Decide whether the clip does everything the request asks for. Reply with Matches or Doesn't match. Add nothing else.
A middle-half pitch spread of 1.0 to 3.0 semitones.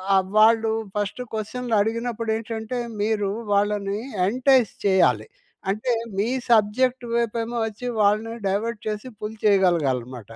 Matches